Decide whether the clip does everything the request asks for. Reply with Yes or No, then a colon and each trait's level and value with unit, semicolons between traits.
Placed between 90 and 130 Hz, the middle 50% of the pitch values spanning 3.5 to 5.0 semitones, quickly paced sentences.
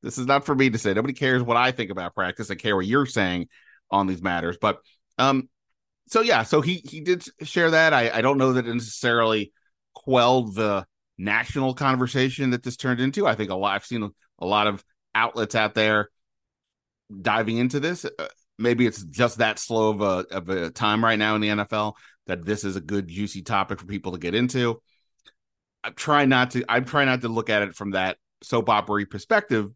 Yes: low, 115 Hz; average, 4.0 semitones; fast, 215 wpm